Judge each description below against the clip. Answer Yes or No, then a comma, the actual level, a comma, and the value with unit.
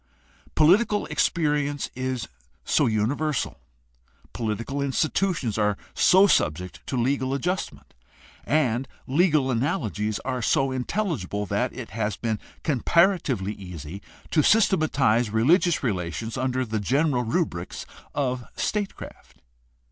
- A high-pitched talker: No, low, 130 Hz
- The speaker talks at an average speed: No, slow, 110 wpm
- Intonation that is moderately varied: No, wide, 6.1 semitones